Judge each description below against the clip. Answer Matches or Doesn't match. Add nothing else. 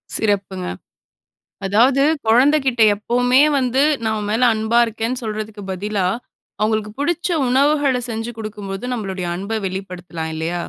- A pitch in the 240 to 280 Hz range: Doesn't match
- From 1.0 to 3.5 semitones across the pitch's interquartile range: Doesn't match